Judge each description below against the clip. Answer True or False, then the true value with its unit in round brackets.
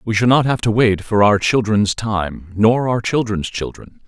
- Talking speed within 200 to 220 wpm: True (205 wpm)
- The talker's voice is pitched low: True (110 Hz)